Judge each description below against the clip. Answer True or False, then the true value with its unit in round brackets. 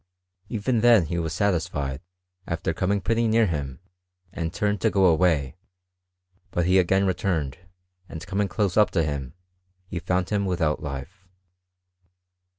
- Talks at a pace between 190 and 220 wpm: False (145 wpm)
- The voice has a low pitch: True (90 Hz)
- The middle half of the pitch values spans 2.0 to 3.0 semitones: False (4.1 semitones)